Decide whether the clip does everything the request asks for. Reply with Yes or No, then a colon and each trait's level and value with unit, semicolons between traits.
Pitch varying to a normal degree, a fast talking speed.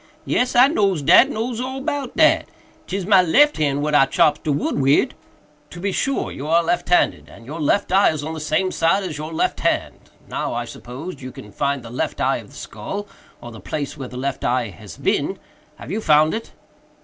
No: wide, 6.3 semitones; fast, 215 wpm